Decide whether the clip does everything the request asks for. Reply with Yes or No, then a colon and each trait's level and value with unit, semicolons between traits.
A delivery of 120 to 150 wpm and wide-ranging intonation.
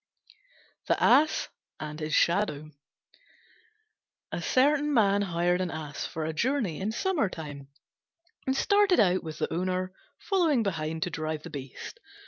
Yes: slow, 135 wpm; wide, 8.5 semitones